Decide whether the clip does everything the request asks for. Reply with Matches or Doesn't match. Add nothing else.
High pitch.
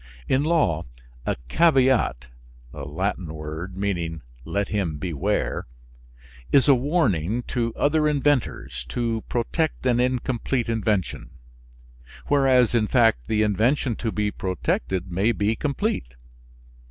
Doesn't match